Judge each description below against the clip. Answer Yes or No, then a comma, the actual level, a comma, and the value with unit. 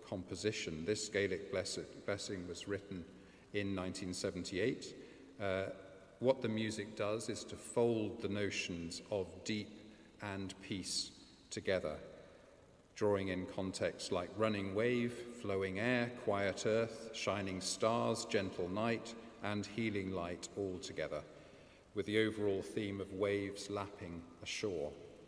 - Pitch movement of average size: No, narrow, 2.3 semitones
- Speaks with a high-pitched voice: No, low, 100 Hz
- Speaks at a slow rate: Yes, slow, 120 wpm